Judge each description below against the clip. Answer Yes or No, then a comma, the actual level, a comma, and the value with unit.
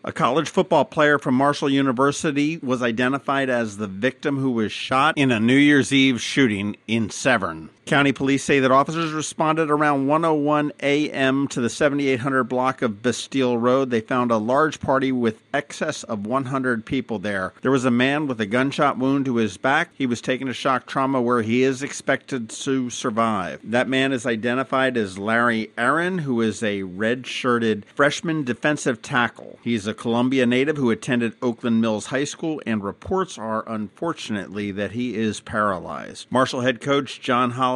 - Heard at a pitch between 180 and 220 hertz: No, low, 130 Hz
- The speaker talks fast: No, average, 175 wpm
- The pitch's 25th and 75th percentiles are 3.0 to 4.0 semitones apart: Yes, average, 3.3 semitones